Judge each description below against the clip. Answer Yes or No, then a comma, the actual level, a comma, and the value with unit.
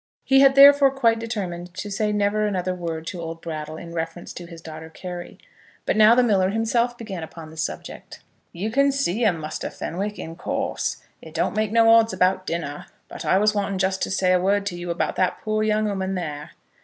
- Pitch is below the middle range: No, high, 190 Hz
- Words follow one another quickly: Yes, fast, 215 wpm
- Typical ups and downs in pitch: Yes, average, 4.2 semitones